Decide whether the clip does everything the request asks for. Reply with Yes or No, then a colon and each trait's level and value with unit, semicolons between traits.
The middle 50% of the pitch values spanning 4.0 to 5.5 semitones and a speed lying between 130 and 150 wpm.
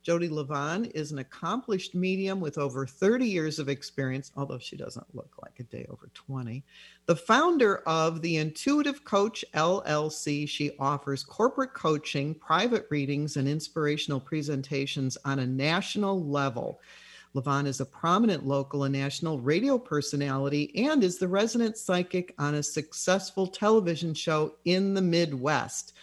Yes: average, 4.8 semitones; average, 145 wpm